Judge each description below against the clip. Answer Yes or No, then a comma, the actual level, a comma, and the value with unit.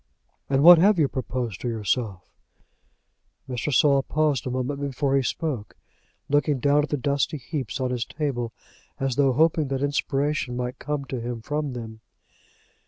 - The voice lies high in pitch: No, low, 135 Hz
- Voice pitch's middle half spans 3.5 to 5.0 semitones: No, average, 3.0 semitones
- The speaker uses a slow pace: No, average, 165 wpm